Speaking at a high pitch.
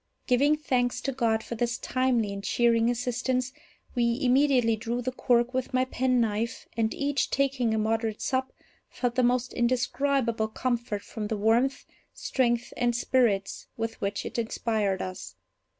Yes: high, 240 Hz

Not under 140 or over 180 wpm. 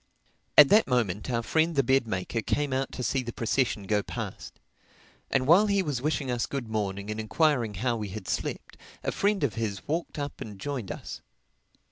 No: average, 195 wpm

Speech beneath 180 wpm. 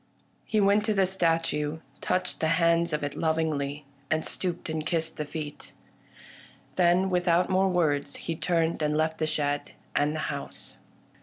Yes: average, 165 wpm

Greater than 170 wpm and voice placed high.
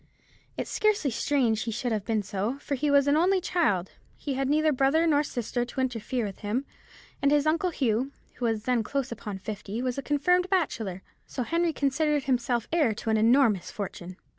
Yes: average, 190 wpm; very high, 260 Hz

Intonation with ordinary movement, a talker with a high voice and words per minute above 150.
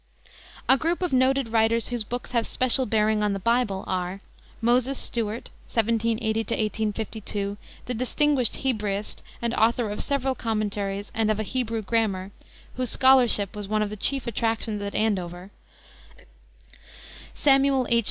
No: average, 3.2 semitones; high, 225 Hz; average, 145 wpm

